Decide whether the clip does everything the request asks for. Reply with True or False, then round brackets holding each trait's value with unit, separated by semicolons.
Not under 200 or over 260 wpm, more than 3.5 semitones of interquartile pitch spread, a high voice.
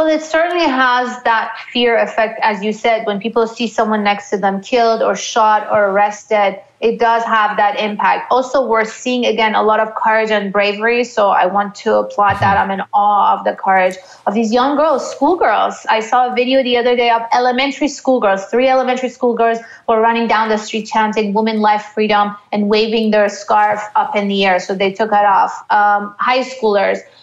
False (205 wpm; 3.0 semitones; 220 Hz)